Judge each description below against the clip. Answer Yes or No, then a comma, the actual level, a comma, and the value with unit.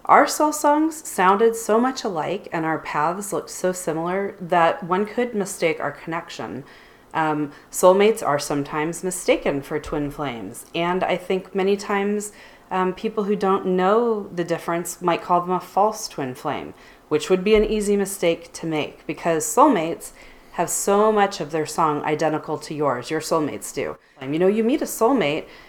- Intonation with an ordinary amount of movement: Yes, average, 4.4 semitones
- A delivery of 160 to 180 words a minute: Yes, average, 175 wpm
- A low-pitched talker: No, medium, 180 Hz